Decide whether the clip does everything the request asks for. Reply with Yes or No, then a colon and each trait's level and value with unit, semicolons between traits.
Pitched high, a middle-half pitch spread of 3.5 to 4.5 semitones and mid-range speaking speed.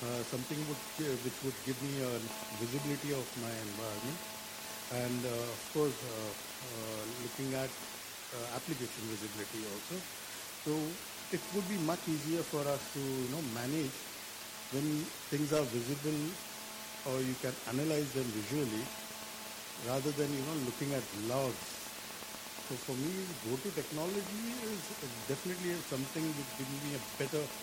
No: low, 135 Hz; average, 4.0 semitones; average, 150 wpm